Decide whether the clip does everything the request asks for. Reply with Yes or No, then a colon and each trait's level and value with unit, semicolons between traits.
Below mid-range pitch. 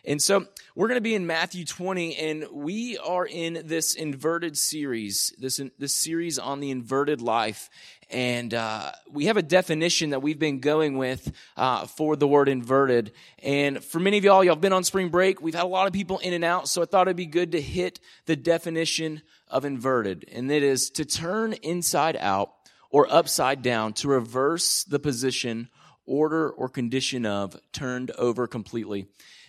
No: medium, 150 Hz